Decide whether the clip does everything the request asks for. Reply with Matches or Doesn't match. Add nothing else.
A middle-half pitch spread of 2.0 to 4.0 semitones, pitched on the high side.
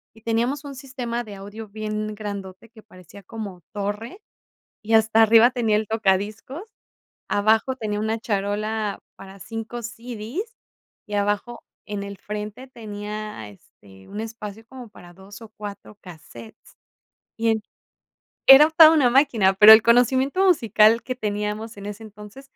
Matches